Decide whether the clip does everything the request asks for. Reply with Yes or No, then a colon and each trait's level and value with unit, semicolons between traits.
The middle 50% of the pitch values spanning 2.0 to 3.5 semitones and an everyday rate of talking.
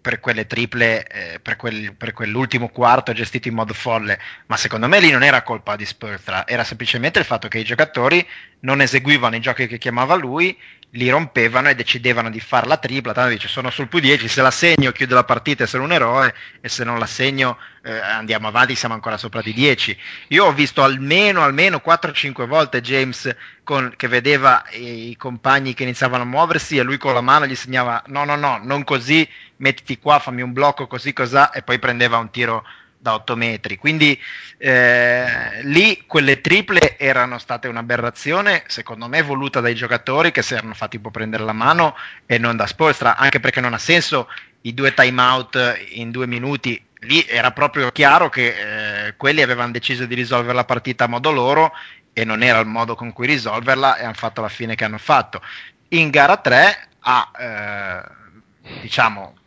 No: average, 2.9 semitones; fast, 195 wpm